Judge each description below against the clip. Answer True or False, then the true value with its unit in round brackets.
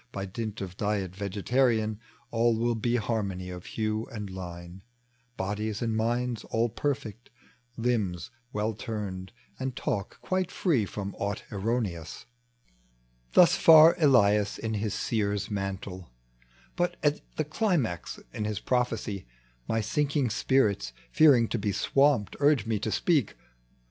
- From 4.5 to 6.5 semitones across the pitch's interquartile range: False (3.6 semitones)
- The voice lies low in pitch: True (110 Hz)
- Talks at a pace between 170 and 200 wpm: False (135 wpm)